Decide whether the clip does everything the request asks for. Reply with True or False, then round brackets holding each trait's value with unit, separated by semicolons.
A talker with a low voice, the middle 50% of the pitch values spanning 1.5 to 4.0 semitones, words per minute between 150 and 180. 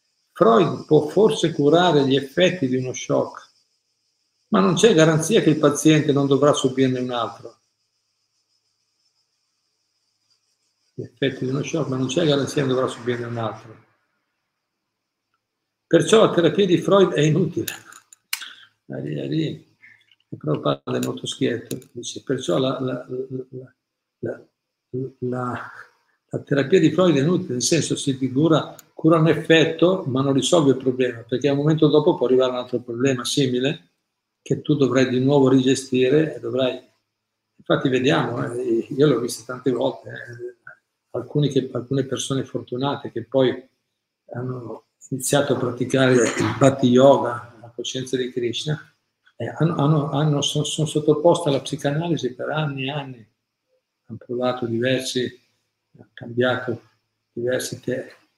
False (130 Hz; 3.4 semitones; 140 wpm)